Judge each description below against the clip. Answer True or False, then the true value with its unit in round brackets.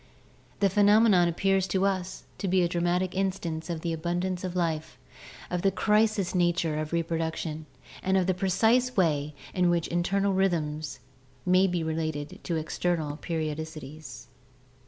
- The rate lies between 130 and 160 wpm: True (150 wpm)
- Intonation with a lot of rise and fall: False (3.0 semitones)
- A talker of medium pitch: True (175 Hz)